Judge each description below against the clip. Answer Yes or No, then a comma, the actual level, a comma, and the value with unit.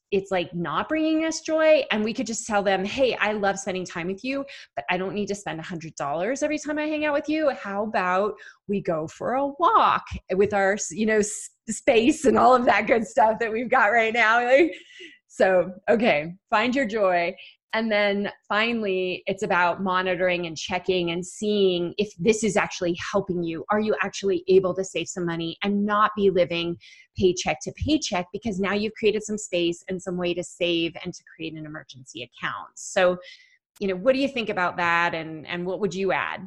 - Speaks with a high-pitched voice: Yes, high, 195 Hz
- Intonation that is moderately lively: Yes, average, 3.8 semitones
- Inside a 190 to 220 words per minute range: Yes, fast, 205 wpm